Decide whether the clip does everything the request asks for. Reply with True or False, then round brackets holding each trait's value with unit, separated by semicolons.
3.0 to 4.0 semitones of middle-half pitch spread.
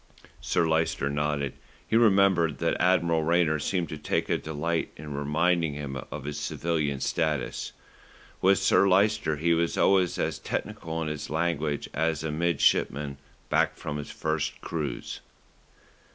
False (2.6 semitones)